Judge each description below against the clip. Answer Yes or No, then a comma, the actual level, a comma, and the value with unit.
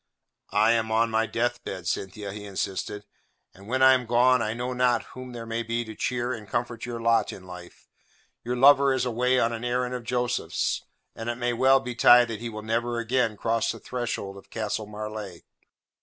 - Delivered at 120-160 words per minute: No, average, 200 wpm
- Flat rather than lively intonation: Yes, narrow, 2.3 semitones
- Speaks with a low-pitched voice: Yes, low, 115 Hz